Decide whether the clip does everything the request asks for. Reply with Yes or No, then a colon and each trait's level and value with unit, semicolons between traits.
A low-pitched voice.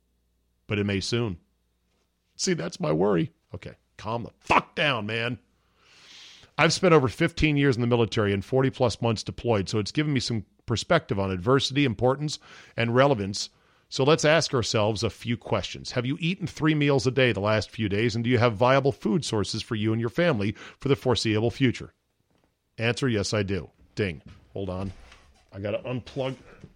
Yes: low, 115 Hz